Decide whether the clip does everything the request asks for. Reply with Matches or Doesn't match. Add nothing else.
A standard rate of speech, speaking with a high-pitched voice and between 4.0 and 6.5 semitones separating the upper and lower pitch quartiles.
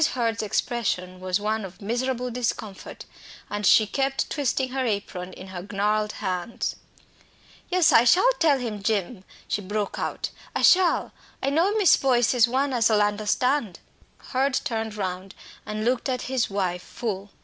Matches